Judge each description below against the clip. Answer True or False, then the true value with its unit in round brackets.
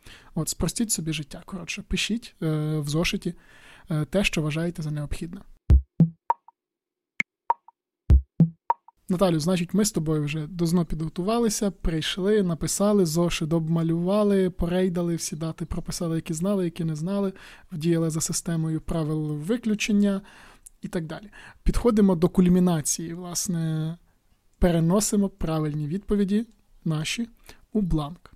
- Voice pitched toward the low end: False (175 Hz)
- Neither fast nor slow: True (115 wpm)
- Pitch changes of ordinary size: True (3.9 semitones)